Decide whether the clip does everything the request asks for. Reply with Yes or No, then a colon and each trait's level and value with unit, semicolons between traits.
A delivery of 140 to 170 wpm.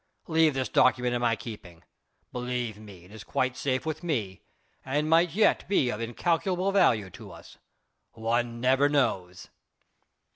Yes: average, 150 wpm